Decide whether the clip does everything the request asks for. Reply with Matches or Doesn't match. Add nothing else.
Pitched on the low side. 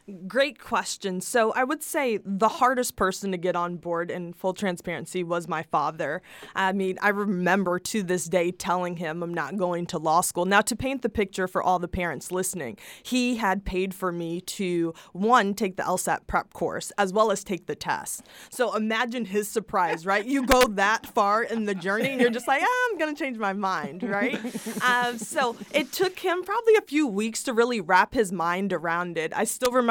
Doesn't match